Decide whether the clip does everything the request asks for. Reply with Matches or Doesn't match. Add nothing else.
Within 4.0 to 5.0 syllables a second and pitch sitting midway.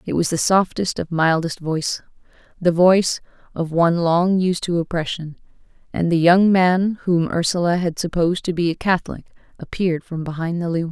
Doesn't match